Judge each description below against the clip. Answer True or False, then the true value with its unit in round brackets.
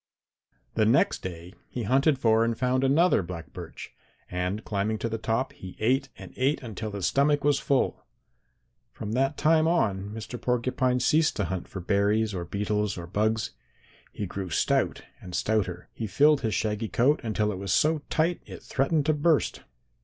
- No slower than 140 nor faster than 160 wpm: False (175 wpm)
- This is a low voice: True (110 Hz)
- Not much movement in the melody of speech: False (5.2 semitones)